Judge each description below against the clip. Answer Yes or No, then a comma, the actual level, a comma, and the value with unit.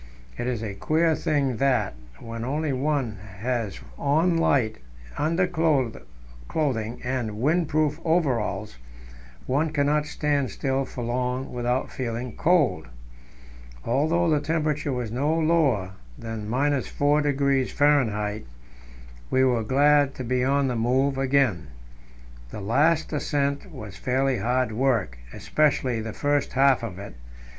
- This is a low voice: Yes, low, 130 Hz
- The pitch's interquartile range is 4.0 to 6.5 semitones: Yes, average, 4.3 semitones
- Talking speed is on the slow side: Yes, slow, 120 wpm